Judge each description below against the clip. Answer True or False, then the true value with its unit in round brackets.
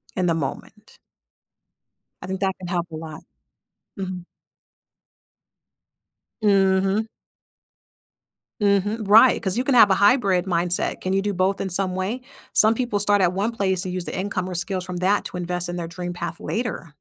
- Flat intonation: True (2.3 semitones)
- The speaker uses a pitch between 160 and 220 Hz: True (190 Hz)